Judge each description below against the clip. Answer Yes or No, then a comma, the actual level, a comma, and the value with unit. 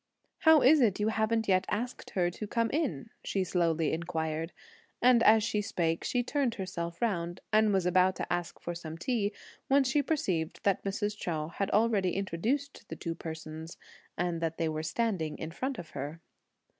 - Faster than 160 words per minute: Yes, average, 180 wpm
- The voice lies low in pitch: No, high, 190 Hz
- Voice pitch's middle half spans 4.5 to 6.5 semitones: Yes, wide, 5.5 semitones